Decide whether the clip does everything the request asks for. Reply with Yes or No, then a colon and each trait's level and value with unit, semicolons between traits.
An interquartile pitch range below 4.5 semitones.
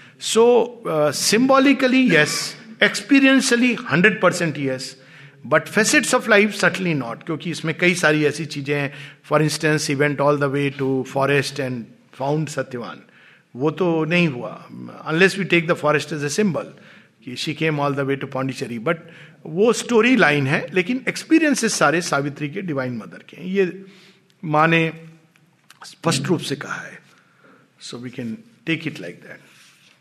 No: average, 5.2 semitones